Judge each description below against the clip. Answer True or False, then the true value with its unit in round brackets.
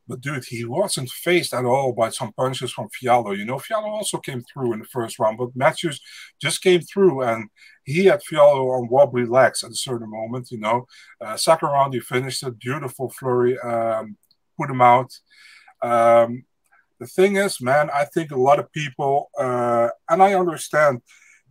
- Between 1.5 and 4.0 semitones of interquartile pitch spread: False (5.2 semitones)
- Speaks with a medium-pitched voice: False (130 Hz)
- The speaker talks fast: False (185 wpm)